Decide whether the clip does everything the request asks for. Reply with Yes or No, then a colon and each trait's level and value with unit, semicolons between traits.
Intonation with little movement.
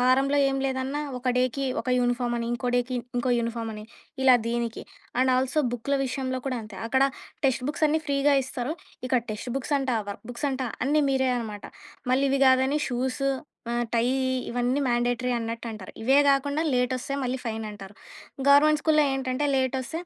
Yes: narrow, 2.1 semitones